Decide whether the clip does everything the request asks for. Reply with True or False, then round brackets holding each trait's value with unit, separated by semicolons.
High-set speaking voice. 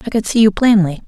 True (210 Hz)